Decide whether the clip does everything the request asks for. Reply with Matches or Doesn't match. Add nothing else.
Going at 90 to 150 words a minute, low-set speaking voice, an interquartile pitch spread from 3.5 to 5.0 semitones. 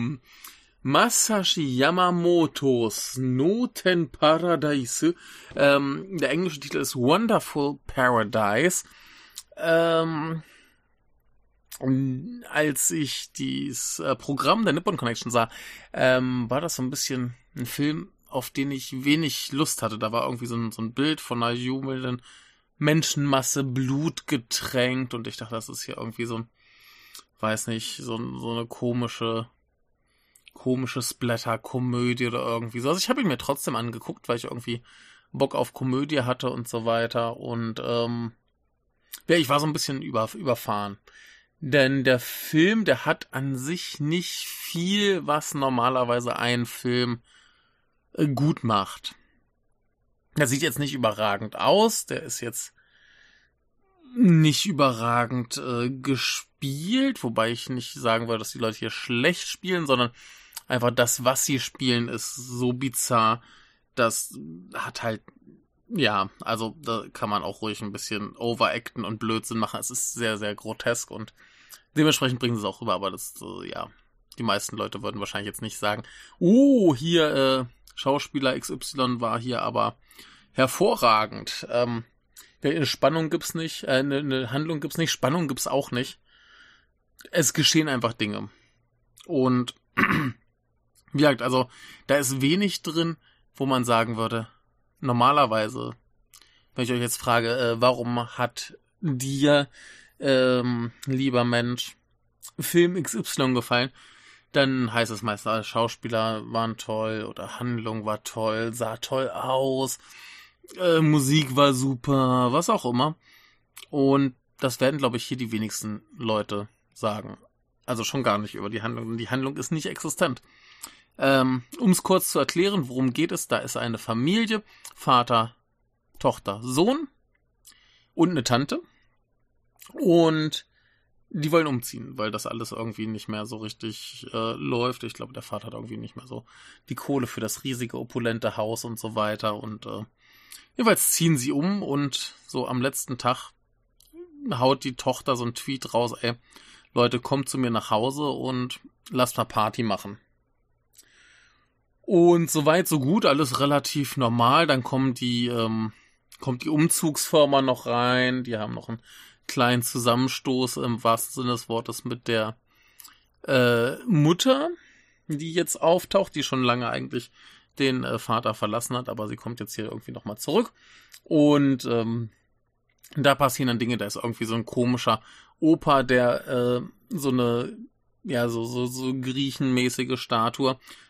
Matches